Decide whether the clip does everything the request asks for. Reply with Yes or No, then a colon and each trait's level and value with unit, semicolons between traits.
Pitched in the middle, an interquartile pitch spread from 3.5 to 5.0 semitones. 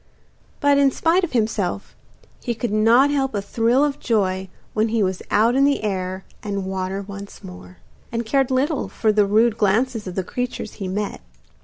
No: high, 215 Hz; average, 4.5 semitones